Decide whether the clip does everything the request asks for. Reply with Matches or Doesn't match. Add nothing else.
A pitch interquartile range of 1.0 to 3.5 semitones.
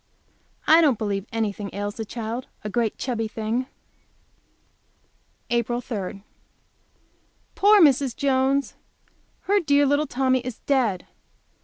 Doesn't match